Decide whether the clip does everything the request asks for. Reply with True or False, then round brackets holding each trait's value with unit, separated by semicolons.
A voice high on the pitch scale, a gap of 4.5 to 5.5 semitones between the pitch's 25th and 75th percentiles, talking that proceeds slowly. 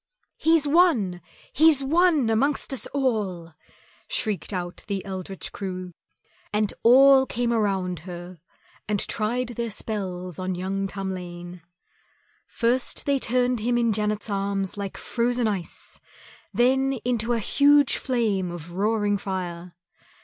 True (210 Hz; 5.1 semitones; 125 wpm)